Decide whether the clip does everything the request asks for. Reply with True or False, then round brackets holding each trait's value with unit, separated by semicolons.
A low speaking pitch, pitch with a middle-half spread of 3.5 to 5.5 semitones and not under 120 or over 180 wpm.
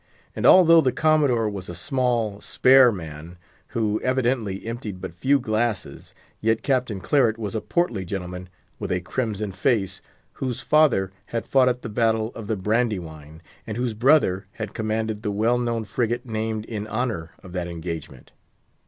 True (110 Hz; 4.3 semitones; 160 wpm)